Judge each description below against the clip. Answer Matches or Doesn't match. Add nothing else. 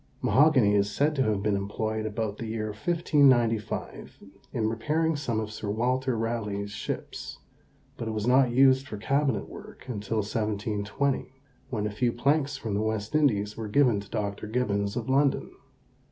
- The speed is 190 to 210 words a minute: Doesn't match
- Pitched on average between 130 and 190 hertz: Doesn't match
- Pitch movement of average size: Matches